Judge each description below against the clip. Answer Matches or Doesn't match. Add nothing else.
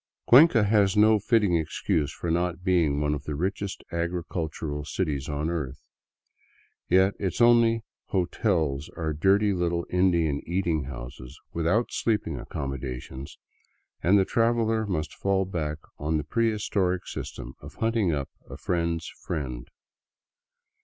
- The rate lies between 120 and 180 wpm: Matches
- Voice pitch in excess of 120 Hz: Doesn't match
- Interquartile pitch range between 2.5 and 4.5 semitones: Doesn't match